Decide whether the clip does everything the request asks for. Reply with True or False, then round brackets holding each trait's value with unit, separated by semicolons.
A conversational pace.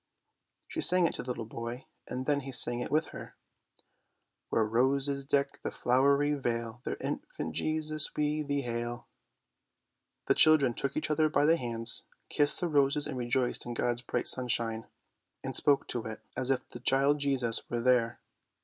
True (185 wpm)